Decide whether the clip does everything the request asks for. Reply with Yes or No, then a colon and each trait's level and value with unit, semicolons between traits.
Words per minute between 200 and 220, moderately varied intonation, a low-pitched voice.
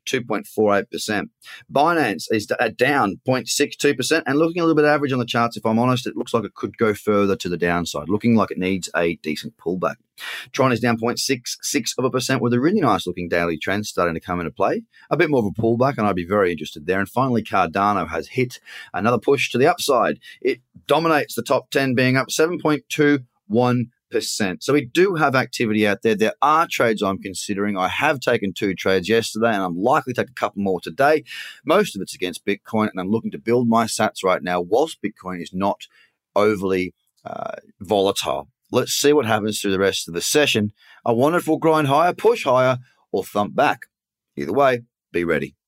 Yes: fast, 205 wpm; average, 4.9 semitones; low, 115 Hz